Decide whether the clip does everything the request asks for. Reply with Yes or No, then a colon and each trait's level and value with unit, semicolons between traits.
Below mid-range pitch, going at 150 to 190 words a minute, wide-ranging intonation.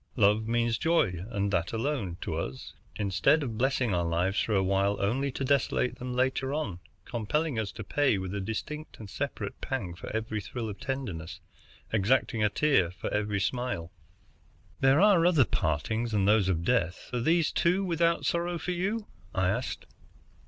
Yes: low, 115 Hz; average, 175 wpm; wide, 6.1 semitones